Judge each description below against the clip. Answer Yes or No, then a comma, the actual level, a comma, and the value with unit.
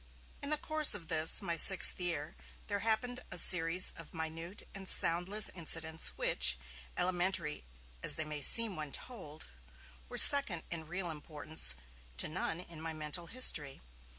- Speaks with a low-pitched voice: No, medium, 170 Hz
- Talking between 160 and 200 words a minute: No, average, 150 wpm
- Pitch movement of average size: Yes, average, 3.5 semitones